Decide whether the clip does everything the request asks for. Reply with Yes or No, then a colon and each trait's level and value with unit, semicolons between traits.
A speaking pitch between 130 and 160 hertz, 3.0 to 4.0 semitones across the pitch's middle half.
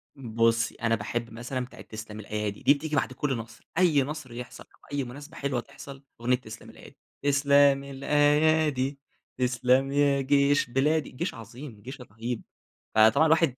Yes: low, 135 Hz; average, 3.3 semitones